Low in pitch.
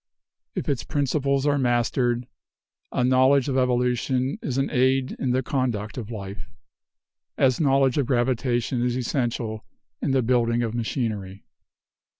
Yes: low, 125 Hz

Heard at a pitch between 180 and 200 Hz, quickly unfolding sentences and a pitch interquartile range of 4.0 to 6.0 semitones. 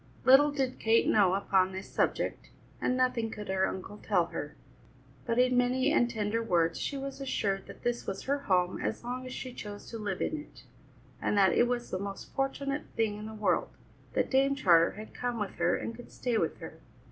No: high, 225 Hz; fast, 210 wpm; average, 4.6 semitones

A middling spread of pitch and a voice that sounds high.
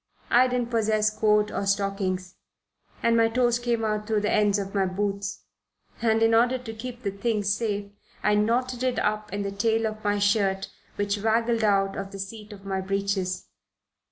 No: narrow, 2.3 semitones; high, 210 Hz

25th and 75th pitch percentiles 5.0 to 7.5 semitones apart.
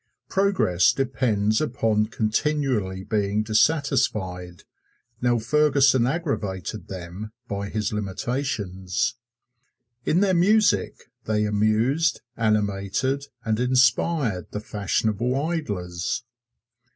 Yes: average, 5.3 semitones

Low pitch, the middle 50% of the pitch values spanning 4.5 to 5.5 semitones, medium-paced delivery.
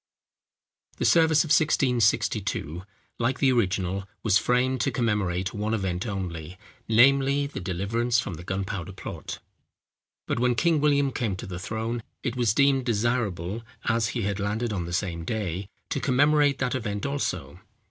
Yes: low, 110 Hz; average, 5.1 semitones; average, 160 wpm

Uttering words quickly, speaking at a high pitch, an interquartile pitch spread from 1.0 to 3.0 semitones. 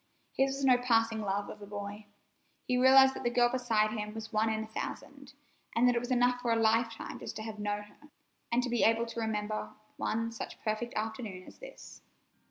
Yes: fast, 215 wpm; high, 225 Hz; narrow, 2.5 semitones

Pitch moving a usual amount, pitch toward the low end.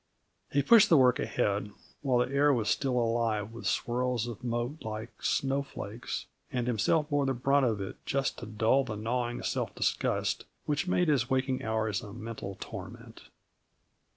Yes: average, 3.6 semitones; low, 120 Hz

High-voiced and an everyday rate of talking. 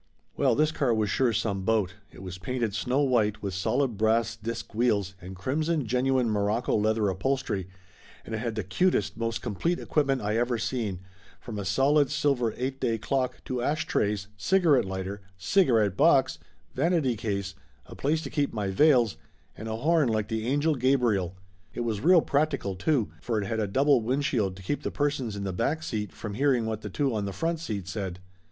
No: low, 115 Hz; average, 195 wpm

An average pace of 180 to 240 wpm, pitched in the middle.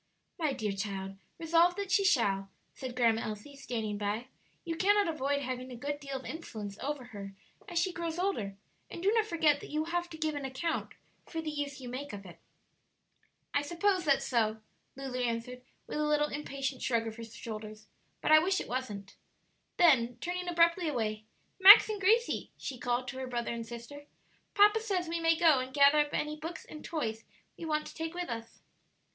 No: average, 200 wpm; very high, 280 Hz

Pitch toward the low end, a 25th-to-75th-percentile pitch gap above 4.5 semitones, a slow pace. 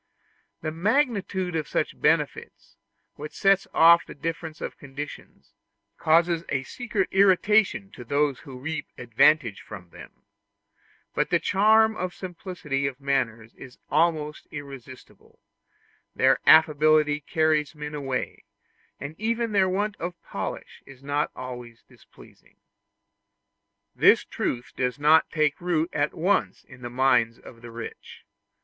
No: medium, 150 Hz; average, 4.9 semitones; slow, 130 wpm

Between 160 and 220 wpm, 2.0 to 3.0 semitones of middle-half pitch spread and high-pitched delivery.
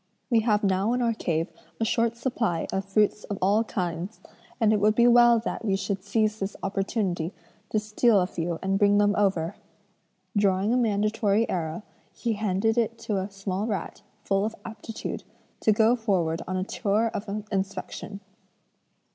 Yes: average, 170 wpm; narrow, 2.6 semitones; high, 205 Hz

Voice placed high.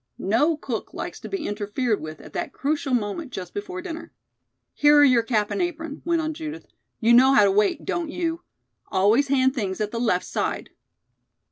Yes: very high, 265 Hz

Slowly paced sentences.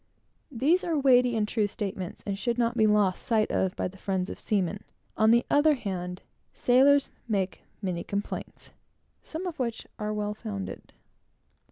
No: average, 165 wpm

